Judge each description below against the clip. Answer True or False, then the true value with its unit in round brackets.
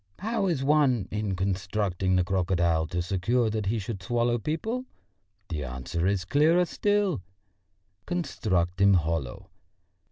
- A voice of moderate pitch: False (100 Hz)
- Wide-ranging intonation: True (7.8 semitones)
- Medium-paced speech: False (130 wpm)